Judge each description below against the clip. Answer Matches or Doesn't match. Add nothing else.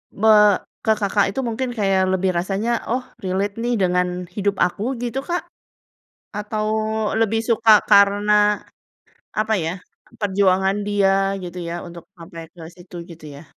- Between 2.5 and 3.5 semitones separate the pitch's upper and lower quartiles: Matches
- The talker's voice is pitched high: Matches